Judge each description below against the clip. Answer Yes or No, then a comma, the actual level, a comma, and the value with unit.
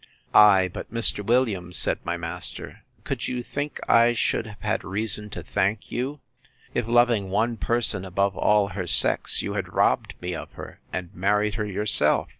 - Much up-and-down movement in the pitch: No, average, 3.6 semitones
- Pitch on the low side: Yes, low, 105 Hz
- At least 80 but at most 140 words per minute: No, average, 175 wpm